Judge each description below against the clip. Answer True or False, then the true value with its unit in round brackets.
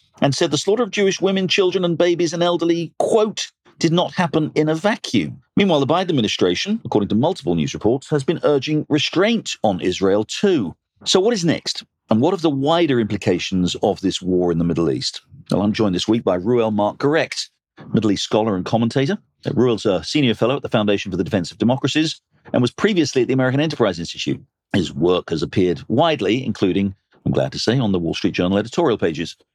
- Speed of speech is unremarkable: False (210 wpm)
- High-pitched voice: False (135 Hz)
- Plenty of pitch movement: True (8.6 semitones)